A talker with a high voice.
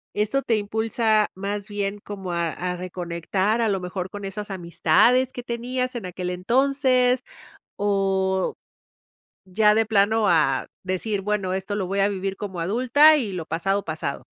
Yes: high, 200 Hz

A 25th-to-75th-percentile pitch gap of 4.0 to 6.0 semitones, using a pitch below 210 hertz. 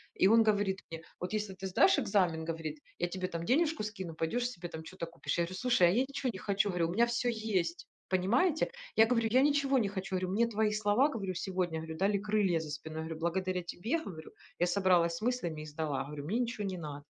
Yes: average, 4.8 semitones; high, 190 Hz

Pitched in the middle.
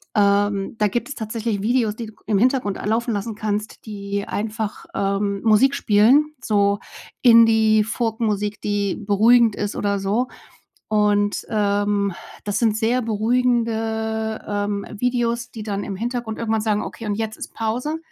No: high, 215 Hz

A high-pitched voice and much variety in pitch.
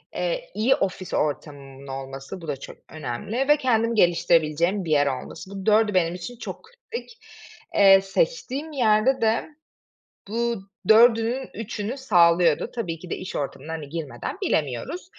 Yes: high, 195 Hz; wide, 7.2 semitones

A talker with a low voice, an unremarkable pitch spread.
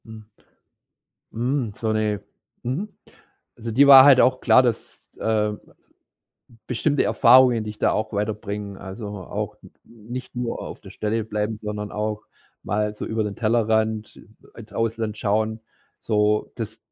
No: low, 110 Hz; narrow, 1.8 semitones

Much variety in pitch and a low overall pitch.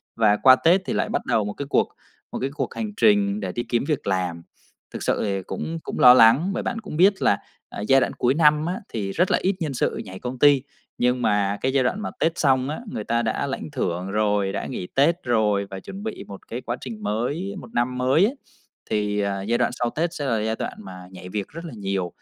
Yes: wide, 6.6 semitones; low, 125 Hz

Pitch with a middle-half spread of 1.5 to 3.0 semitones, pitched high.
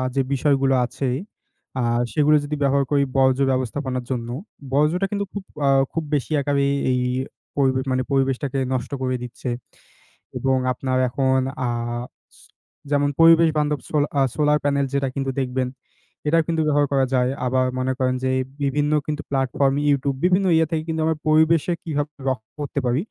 No: narrow, 2.4 semitones; medium, 140 Hz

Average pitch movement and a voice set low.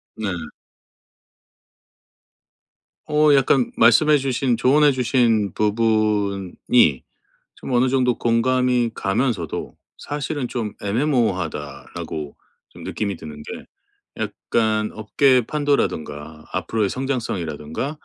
Yes: average, 4.8 semitones; low, 115 Hz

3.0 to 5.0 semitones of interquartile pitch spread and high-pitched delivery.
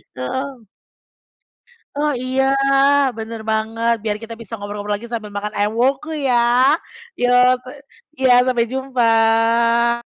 No: narrow, 2.4 semitones; high, 235 Hz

